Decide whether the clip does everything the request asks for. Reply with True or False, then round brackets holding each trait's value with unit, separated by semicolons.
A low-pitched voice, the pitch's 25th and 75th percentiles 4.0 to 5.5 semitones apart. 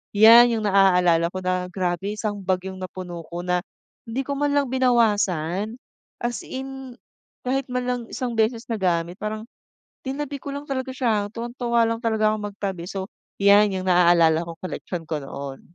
False (210 Hz; 5.1 semitones)